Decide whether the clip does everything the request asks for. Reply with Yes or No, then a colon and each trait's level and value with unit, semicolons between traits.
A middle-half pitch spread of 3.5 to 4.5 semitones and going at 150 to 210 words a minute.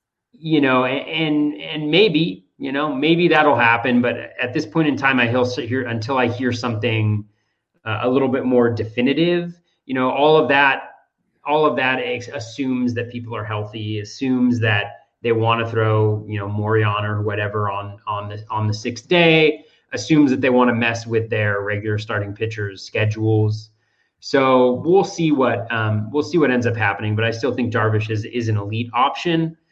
Yes: average, 4.2 semitones; average, 190 wpm